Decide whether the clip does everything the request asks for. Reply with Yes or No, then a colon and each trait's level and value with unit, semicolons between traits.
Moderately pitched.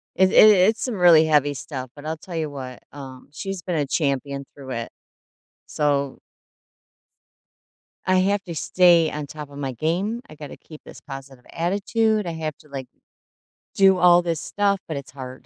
Yes: medium, 155 Hz